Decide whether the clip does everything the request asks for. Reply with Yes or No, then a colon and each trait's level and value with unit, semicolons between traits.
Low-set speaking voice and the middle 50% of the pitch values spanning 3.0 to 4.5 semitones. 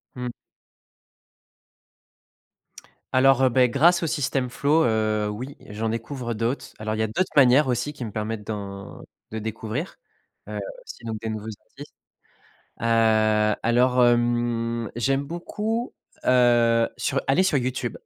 Yes: low, 120 Hz; average, 3.4 semitones